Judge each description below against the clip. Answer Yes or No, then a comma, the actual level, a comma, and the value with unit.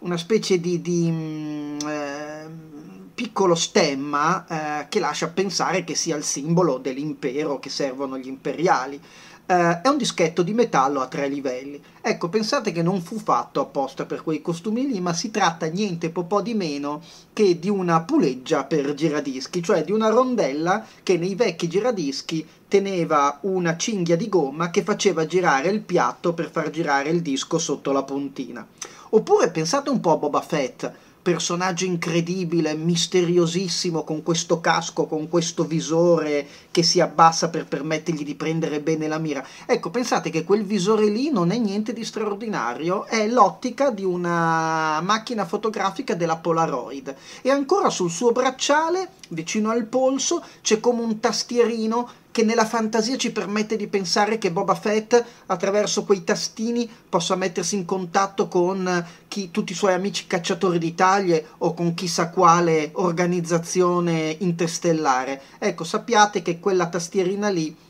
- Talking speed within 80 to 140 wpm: No, average, 155 wpm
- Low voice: No, medium, 180 Hz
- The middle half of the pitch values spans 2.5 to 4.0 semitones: No, average, 4.5 semitones